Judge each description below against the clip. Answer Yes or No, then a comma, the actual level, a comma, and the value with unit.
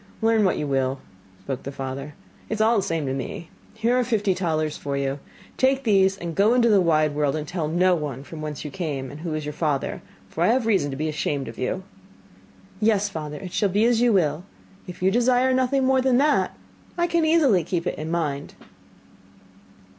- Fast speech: Yes, fast, 215 wpm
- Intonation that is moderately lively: No, wide, 7.1 semitones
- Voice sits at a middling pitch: Yes, medium, 175 Hz